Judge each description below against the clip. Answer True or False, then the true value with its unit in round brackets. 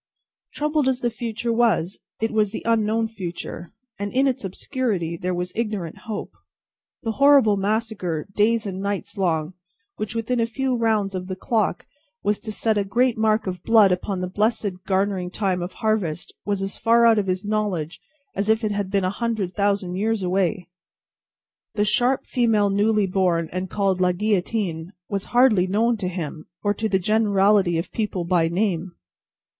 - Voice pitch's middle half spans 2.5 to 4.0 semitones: True (3.3 semitones)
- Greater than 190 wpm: False (175 wpm)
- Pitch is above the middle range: True (205 Hz)